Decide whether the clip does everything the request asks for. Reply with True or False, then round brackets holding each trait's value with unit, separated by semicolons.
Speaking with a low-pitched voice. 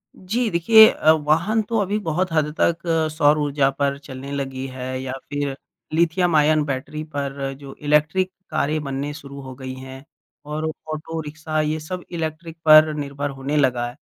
False (150 Hz)